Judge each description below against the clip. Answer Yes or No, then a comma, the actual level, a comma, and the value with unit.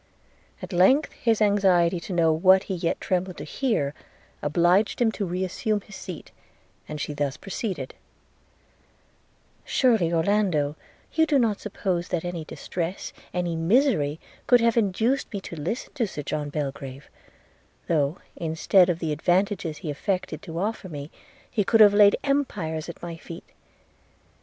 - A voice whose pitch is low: No, medium, 180 Hz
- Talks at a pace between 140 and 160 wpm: Yes, average, 150 wpm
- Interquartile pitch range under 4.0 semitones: No, average, 4.4 semitones